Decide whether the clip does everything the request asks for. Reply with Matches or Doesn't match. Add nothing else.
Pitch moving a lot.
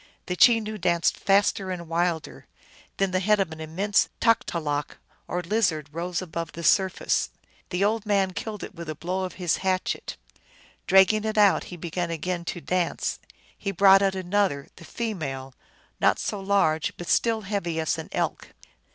Doesn't match